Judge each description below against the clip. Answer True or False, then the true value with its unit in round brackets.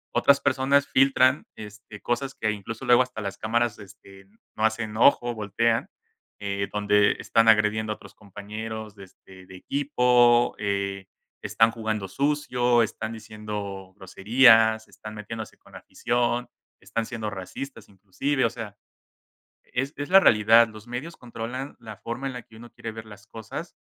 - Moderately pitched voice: False (110 Hz)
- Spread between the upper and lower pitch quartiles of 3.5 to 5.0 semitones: False (2.7 semitones)